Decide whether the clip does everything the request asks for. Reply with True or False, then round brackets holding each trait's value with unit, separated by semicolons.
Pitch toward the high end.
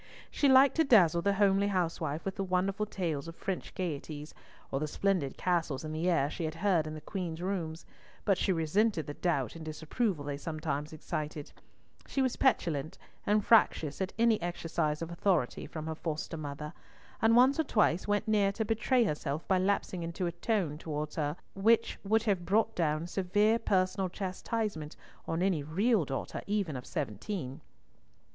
False (175 Hz)